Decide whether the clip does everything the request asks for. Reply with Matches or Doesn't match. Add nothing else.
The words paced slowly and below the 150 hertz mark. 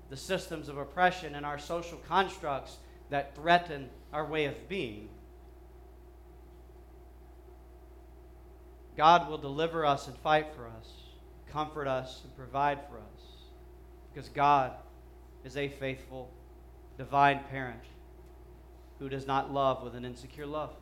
Matches